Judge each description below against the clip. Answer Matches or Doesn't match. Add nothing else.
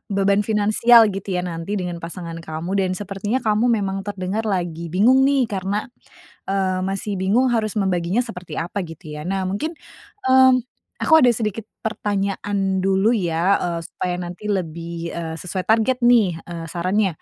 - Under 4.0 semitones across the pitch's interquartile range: Matches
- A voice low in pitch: Doesn't match